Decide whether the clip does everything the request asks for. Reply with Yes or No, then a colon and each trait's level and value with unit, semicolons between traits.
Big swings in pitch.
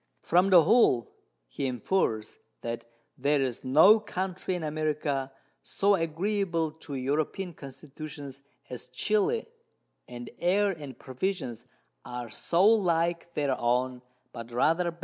Yes: wide, 5.9 semitones